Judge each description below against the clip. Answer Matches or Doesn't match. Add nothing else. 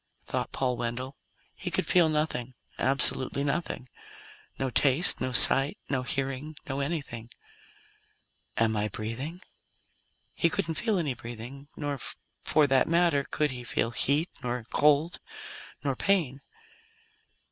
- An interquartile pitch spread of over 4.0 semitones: Doesn't match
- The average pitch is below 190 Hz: Matches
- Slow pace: Matches